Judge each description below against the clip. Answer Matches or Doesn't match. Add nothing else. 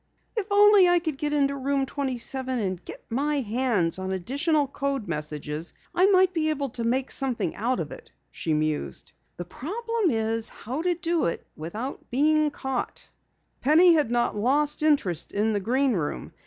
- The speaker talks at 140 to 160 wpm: Doesn't match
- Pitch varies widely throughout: Matches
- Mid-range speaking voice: Doesn't match